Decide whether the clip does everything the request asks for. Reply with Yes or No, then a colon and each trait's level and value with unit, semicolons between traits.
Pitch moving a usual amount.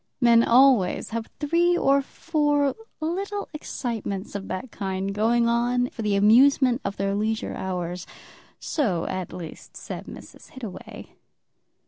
No: wide, 5.8 semitones